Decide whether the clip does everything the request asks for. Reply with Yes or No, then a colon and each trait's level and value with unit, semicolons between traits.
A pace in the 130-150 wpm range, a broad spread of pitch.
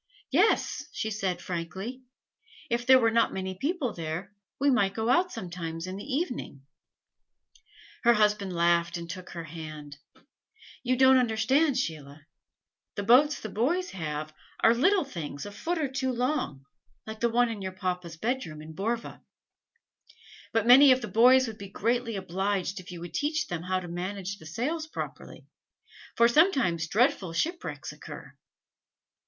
No: average, 165 wpm; wide, 6.7 semitones